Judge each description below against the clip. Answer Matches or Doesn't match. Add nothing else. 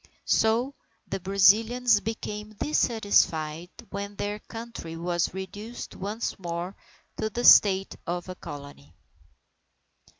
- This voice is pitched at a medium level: Doesn't match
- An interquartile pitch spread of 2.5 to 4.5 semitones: Matches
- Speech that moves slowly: Matches